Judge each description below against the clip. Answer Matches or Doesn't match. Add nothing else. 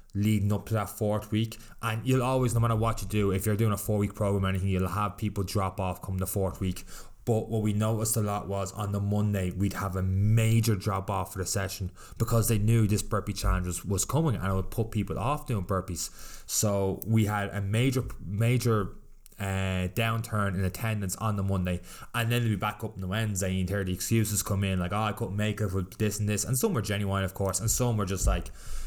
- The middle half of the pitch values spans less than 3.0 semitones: Matches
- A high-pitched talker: Doesn't match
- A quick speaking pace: Matches